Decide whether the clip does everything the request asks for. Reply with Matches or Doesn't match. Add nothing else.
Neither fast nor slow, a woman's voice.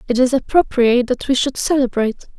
Matches